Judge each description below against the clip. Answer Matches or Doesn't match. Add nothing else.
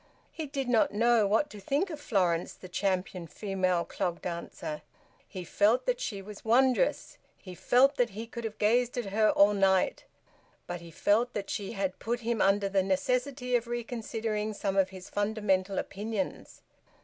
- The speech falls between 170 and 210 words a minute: Matches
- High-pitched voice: Matches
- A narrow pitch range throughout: Doesn't match